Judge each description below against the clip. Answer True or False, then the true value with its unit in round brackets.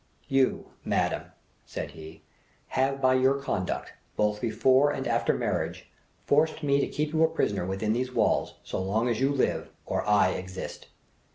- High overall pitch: False (130 Hz)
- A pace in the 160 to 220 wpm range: True (165 wpm)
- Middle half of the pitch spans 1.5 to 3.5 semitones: False (4.9 semitones)